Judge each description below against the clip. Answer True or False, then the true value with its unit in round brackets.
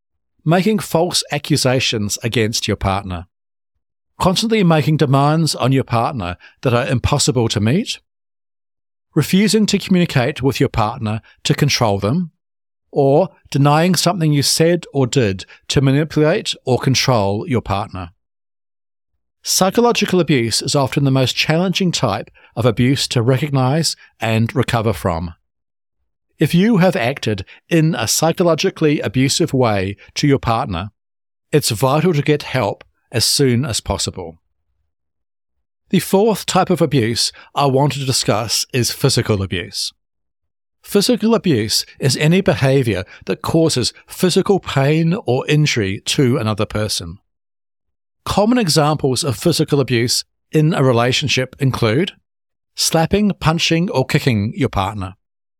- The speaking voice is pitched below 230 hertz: True (135 Hz)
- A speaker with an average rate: False (125 wpm)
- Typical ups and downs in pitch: False (7.0 semitones)